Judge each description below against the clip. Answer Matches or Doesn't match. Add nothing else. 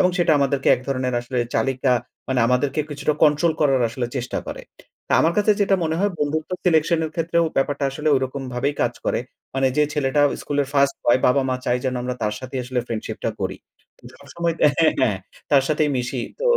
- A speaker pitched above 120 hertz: Matches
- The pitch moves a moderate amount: Matches